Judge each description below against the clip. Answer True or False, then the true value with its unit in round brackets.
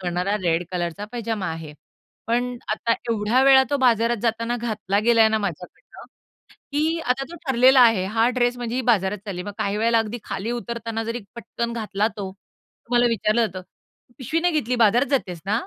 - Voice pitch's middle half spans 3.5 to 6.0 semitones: False (3.1 semitones)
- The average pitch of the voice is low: False (230 Hz)